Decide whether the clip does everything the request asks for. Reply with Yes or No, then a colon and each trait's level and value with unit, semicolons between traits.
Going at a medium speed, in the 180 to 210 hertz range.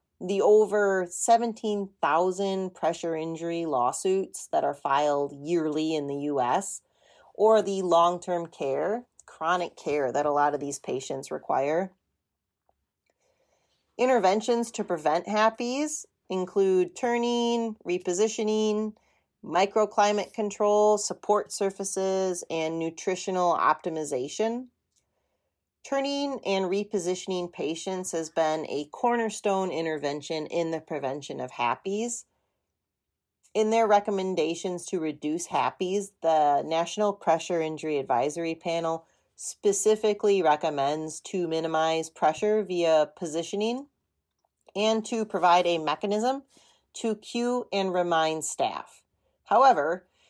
No: slow, 100 wpm; medium, 185 Hz